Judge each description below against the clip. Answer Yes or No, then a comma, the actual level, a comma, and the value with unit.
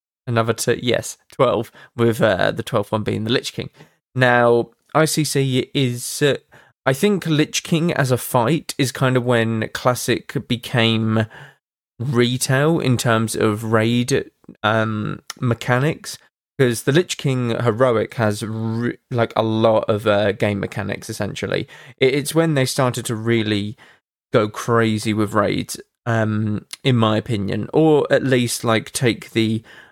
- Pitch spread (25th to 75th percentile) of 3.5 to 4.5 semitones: No, average, 3.0 semitones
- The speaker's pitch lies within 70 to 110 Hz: No, low, 120 Hz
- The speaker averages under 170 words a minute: Yes, average, 145 wpm